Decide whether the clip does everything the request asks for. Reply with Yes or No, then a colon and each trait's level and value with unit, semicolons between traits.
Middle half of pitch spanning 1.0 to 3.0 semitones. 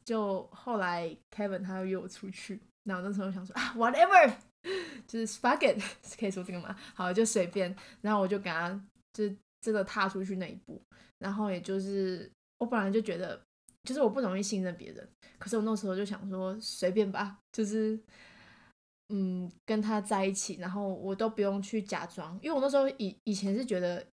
Yes: narrow, 2.6 semitones